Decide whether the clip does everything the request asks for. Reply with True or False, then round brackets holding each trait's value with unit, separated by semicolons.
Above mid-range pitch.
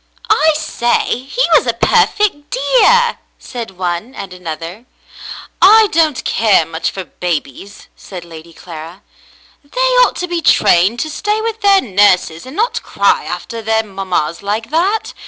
True (225 Hz)